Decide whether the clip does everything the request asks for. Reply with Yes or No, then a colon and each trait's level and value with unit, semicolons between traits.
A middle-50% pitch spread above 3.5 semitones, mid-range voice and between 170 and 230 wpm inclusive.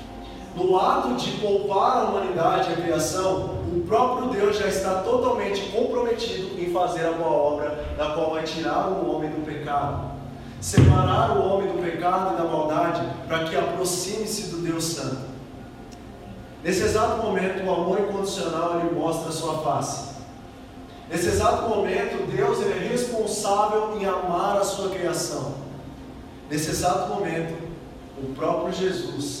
No: average, 4.2 semitones; medium, 170 Hz; average, 145 wpm